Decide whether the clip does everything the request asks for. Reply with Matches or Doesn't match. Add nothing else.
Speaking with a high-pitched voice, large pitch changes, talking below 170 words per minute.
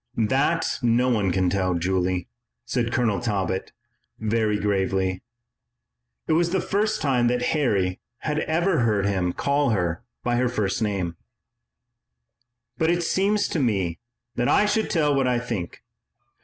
Doesn't match